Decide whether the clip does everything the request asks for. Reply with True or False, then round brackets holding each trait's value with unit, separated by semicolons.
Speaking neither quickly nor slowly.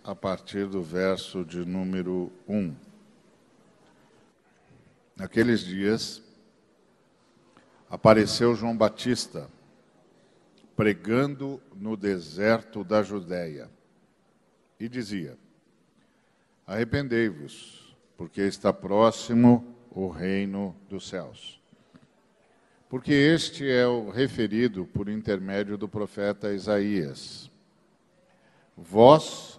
False (75 wpm)